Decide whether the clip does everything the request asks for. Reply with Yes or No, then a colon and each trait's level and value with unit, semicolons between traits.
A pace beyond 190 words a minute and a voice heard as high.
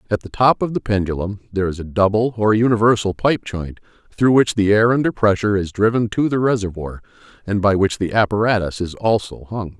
No: average, 200 wpm; low, 105 Hz